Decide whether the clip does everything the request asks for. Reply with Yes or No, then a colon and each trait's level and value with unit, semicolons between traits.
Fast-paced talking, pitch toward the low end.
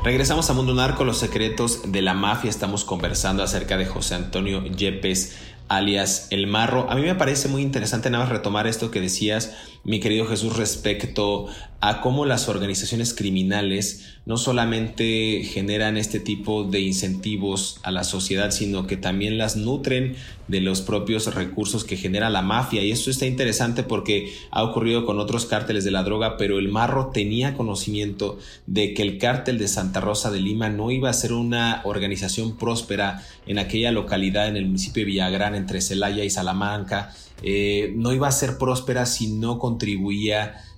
No: average, 175 wpm; low, 105 Hz